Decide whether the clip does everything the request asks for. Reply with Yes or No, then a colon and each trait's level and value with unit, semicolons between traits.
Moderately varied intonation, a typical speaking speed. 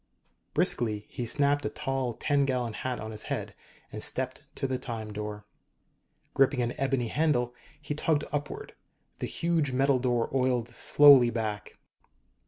Yes: average, 3.4 semitones; average, 150 wpm